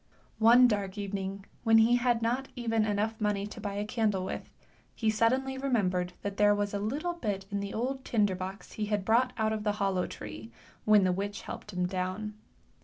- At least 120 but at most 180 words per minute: No, average, 200 wpm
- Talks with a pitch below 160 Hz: No, high, 210 Hz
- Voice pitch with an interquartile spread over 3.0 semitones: No, narrow, 2.5 semitones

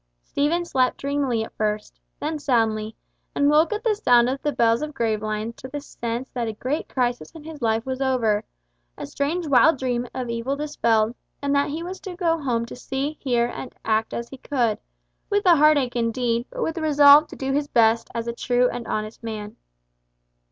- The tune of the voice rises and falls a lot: No, average, 4.2 semitones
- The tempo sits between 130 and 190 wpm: No, average, 200 wpm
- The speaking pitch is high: Yes, very high, 255 Hz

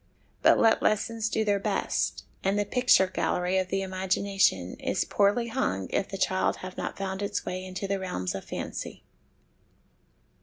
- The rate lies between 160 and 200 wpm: Yes, average, 165 wpm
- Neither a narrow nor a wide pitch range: No, narrow, 1.8 semitones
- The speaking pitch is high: Yes, high, 195 Hz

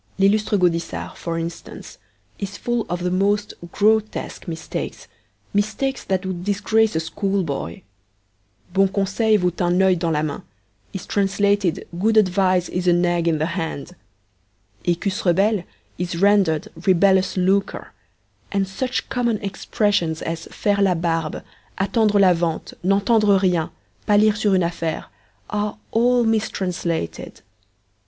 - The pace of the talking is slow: Yes, slow, 130 wpm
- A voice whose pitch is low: No, high, 190 Hz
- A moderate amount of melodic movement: Yes, average, 3.0 semitones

